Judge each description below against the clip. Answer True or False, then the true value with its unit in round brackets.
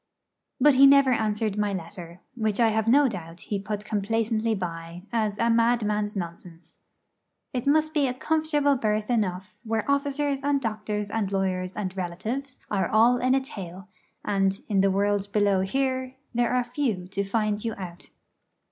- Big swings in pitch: False (4.4 semitones)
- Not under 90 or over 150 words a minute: False (165 wpm)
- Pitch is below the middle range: False (215 Hz)